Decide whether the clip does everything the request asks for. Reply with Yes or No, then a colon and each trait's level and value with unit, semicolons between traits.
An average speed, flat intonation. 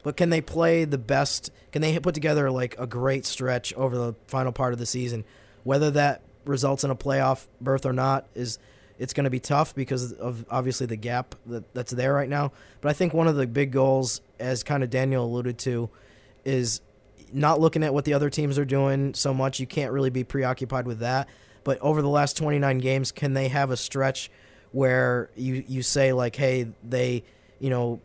No: fast, 210 wpm; narrow, 2.1 semitones